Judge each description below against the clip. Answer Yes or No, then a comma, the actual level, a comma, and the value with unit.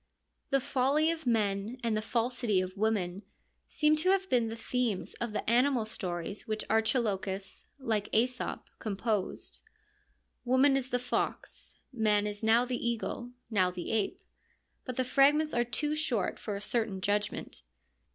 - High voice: Yes, high, 230 Hz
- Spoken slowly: No, average, 155 wpm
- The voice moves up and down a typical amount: Yes, average, 3.6 semitones